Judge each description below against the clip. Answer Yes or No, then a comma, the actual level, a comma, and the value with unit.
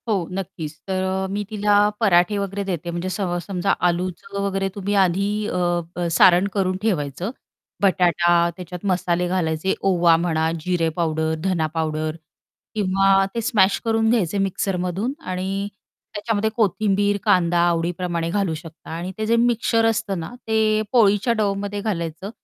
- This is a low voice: No, high, 190 Hz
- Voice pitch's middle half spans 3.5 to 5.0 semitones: No, average, 2.9 semitones